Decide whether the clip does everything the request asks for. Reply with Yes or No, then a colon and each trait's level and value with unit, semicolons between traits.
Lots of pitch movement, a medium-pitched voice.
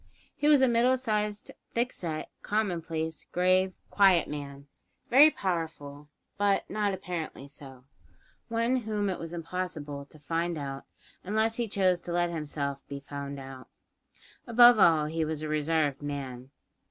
Yes: wide, 6.2 semitones; medium, 170 Hz